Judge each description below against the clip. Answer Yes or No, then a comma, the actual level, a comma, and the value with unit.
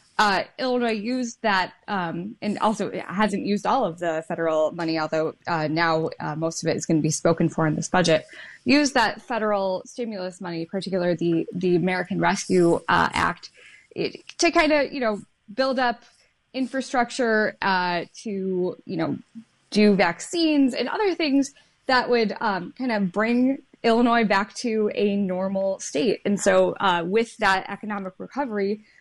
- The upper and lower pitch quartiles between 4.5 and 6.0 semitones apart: Yes, wide, 5.4 semitones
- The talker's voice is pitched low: No, high, 205 Hz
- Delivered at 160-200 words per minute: Yes, average, 165 wpm